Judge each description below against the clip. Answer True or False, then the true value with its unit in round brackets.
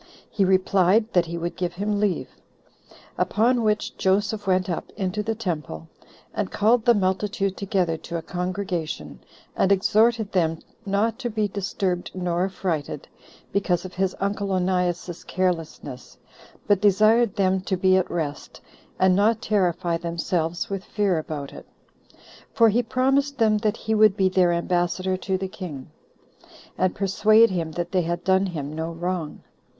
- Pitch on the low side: False (190 Hz)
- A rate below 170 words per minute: True (155 wpm)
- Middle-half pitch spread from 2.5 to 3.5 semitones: True (3.0 semitones)